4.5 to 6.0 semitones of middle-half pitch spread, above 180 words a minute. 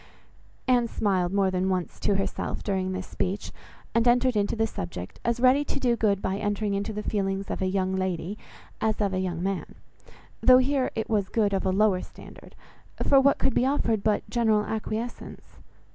No: average, 3.5 semitones; average, 190 wpm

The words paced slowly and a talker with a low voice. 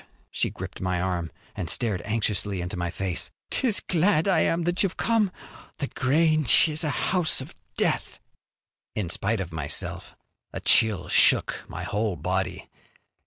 No: average, 155 wpm; low, 110 Hz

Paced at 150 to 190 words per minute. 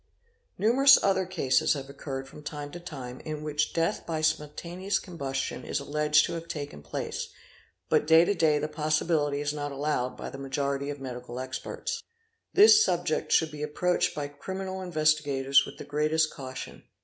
Yes: average, 170 wpm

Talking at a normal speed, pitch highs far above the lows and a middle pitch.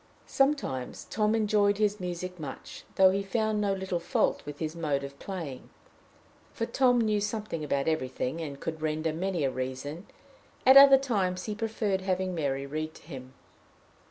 Yes: average, 165 wpm; wide, 5.8 semitones; medium, 180 Hz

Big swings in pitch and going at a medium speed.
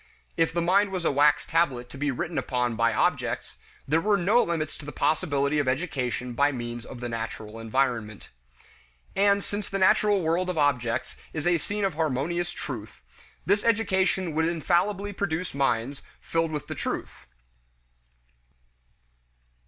Yes: wide, 6.1 semitones; average, 155 wpm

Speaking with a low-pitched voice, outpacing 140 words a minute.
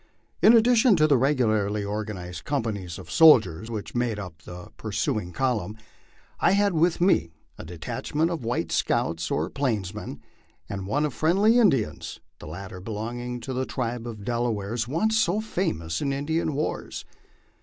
Yes: low, 120 Hz; average, 155 wpm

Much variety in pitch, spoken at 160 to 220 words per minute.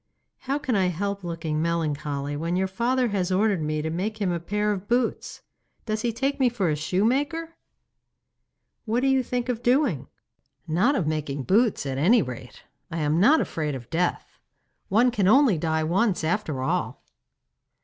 Yes: wide, 7.1 semitones; average, 175 wpm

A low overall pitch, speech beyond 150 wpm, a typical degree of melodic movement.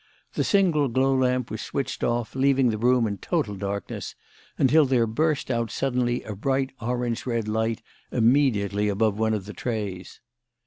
Yes: low, 120 Hz; average, 165 wpm; average, 3.5 semitones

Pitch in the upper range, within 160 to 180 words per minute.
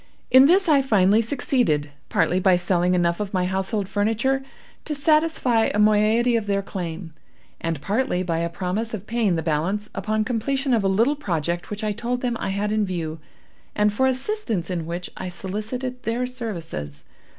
Yes: high, 210 Hz; average, 175 wpm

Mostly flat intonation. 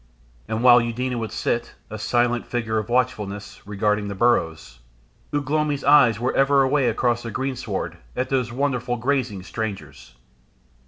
No: average, 3.3 semitones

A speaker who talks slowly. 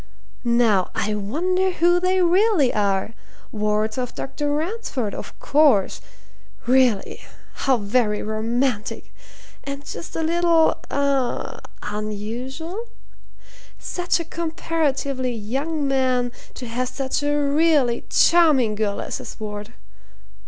Yes: slow, 110 wpm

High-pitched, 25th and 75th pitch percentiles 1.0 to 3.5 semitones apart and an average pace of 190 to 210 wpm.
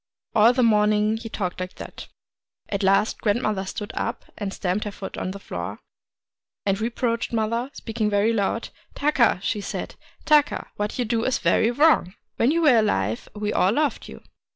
Yes: high, 215 Hz; average, 3.1 semitones; average, 195 wpm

